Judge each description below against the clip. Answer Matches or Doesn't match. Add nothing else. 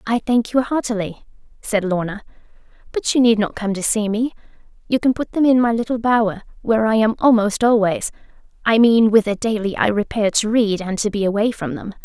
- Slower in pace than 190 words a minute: Doesn't match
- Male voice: Doesn't match